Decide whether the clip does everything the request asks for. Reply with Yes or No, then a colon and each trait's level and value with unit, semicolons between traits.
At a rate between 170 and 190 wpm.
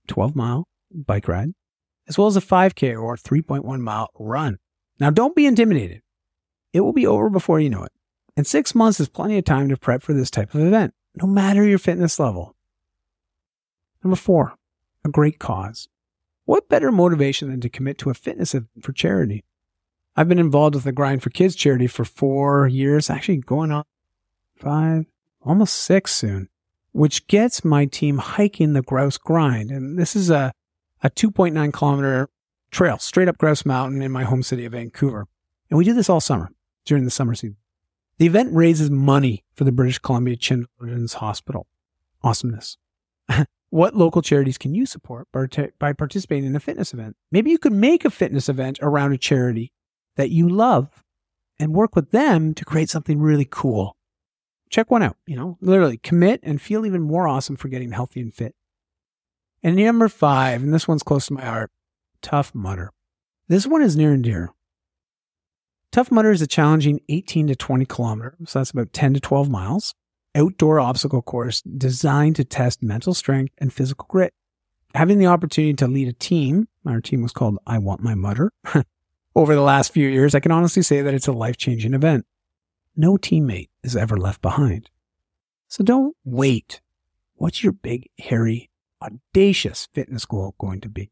Yes: average, 180 wpm